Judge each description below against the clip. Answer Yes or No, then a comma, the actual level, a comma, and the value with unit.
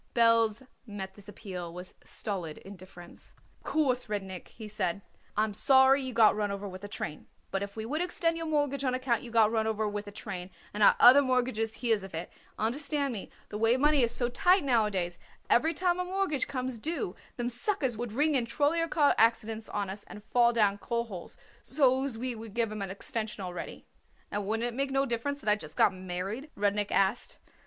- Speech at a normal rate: No, fast, 210 wpm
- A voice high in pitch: Yes, high, 225 Hz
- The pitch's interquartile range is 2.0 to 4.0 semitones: No, average, 4.5 semitones